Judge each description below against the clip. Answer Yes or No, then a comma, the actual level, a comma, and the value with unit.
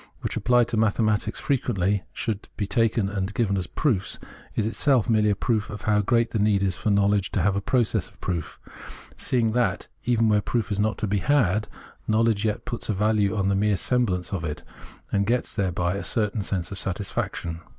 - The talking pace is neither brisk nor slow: No, fast, 215 wpm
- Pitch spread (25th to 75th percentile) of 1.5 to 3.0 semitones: Yes, narrow, 2.5 semitones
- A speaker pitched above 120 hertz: No, low, 105 Hz